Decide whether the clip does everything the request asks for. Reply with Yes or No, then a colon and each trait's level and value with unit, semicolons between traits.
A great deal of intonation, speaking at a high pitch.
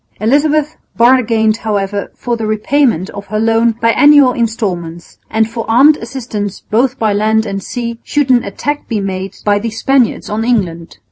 No: average, 3.2 semitones; high, 225 Hz